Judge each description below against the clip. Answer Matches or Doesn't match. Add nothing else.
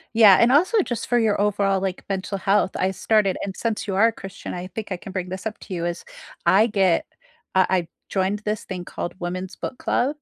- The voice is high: Matches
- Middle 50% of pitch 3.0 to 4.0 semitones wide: Doesn't match